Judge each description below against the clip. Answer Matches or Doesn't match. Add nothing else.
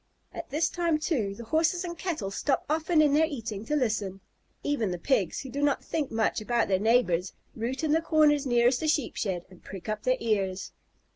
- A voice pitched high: Matches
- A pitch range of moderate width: Doesn't match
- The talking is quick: Matches